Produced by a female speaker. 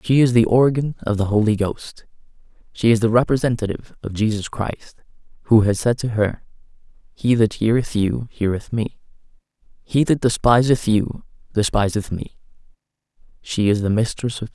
No: male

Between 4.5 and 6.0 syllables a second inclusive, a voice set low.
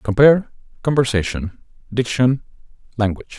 Yes: 5.5 syllables/s; low, 120 Hz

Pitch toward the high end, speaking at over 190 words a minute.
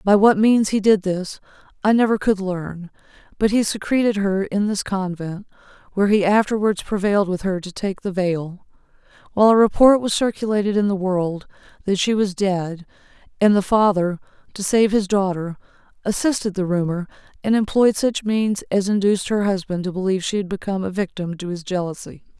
No: high, 195 Hz; average, 180 wpm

